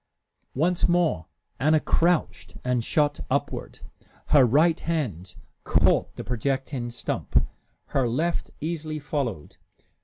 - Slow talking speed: Yes, slow, 110 wpm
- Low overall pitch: No, medium, 145 Hz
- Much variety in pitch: No, average, 4.7 semitones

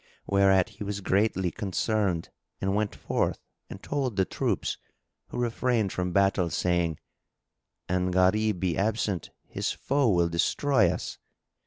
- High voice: No, low, 100 Hz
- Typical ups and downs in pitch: Yes, average, 3.0 semitones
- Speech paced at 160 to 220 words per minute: No, slow, 135 wpm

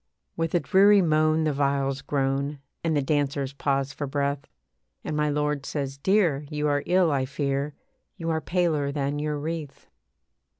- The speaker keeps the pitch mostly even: Yes, narrow, 2.1 semitones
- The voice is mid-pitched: Yes, medium, 145 Hz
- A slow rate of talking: No, average, 165 wpm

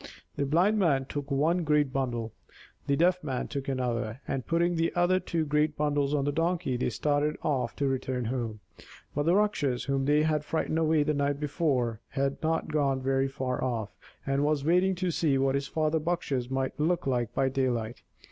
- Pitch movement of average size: Yes, average, 3.1 semitones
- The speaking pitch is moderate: Yes, medium, 145 Hz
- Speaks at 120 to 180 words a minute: No, average, 195 wpm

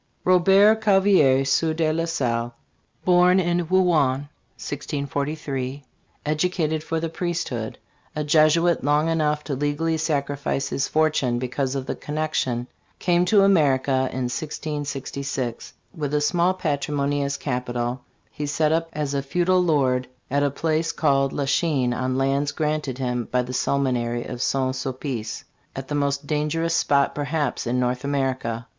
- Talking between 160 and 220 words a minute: No, average, 150 wpm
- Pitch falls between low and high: Yes, medium, 145 Hz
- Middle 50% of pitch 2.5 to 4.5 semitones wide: Yes, average, 3.4 semitones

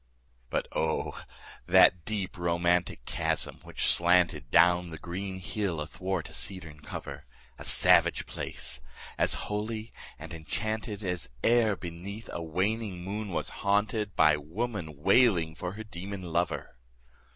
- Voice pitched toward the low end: Yes, very low, 90 Hz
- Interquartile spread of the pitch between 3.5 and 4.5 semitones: Yes, average, 3.9 semitones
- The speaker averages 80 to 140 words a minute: Yes, slow, 135 wpm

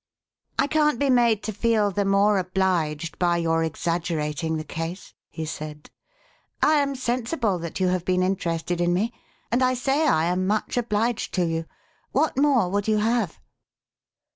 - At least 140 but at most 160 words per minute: No, average, 170 wpm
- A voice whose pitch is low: No, high, 190 Hz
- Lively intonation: Yes, wide, 5.9 semitones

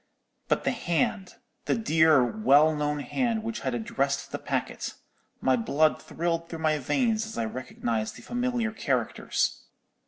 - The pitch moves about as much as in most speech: No, wide, 8.1 semitones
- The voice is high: No, medium, 160 Hz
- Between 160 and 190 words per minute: No, average, 145 wpm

